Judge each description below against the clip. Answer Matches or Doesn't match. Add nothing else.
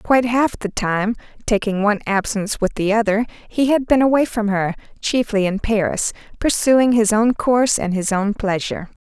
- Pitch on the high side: Matches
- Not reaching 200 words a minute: Matches